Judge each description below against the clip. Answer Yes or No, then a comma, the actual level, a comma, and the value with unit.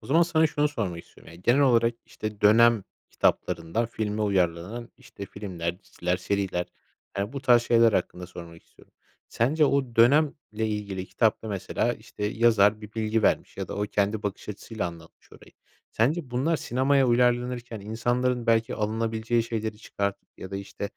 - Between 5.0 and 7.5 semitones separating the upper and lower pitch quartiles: No, average, 3.3 semitones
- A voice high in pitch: No, low, 110 Hz